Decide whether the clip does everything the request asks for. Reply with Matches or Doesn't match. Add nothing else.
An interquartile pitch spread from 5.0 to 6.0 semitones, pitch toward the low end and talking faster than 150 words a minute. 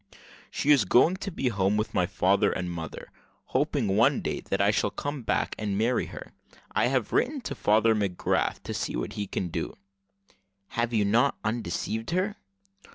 Matches